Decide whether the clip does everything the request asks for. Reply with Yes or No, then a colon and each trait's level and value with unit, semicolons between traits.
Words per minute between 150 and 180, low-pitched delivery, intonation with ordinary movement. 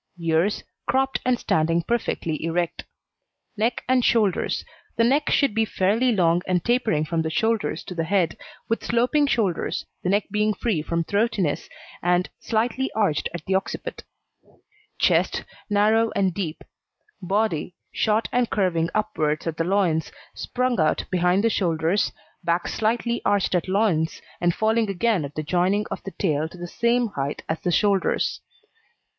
No: average, 155 wpm; high, 195 Hz; average, 5.0 semitones